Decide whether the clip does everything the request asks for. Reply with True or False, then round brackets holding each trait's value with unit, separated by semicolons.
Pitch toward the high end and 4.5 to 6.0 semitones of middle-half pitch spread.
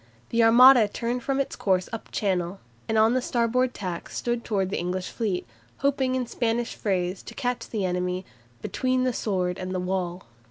True (220 Hz; 5.0 semitones)